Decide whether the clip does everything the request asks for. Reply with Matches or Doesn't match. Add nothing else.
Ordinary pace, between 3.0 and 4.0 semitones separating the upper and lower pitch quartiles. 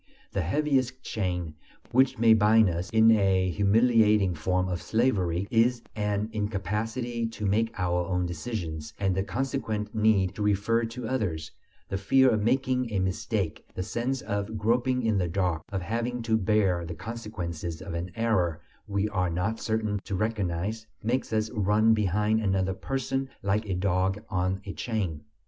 Matches